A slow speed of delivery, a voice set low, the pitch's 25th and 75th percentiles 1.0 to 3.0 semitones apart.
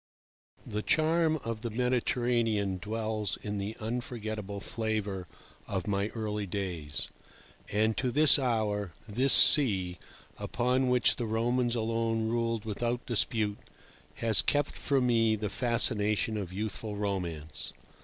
Yes: slow, 125 wpm; low, 110 Hz; average, 2.7 semitones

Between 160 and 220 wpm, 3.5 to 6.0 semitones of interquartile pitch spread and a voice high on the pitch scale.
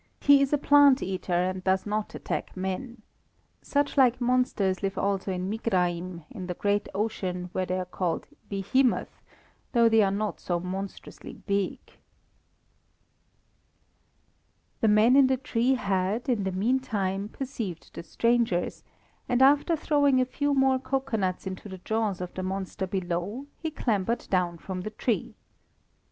No: average, 150 wpm; average, 5.3 semitones; high, 205 Hz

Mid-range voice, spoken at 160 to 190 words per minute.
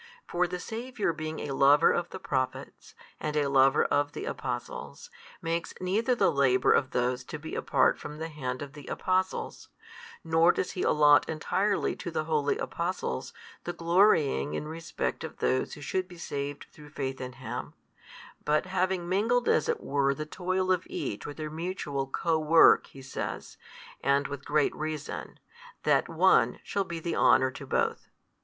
Yes: medium, 155 Hz; average, 175 wpm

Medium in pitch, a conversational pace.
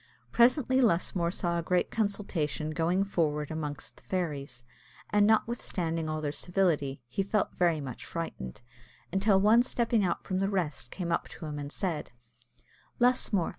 Yes: medium, 175 Hz; average, 155 wpm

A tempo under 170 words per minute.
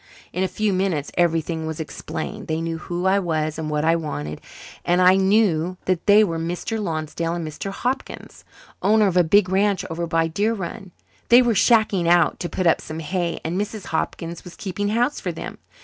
No: average, 200 wpm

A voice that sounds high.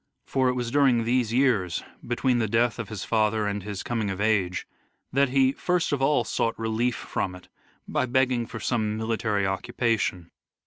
No: low, 115 Hz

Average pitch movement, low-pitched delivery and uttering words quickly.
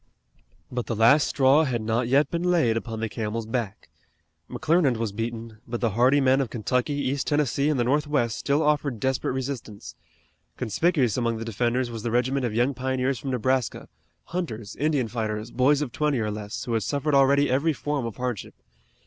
No: average, 3.6 semitones; low, 125 Hz; average, 185 wpm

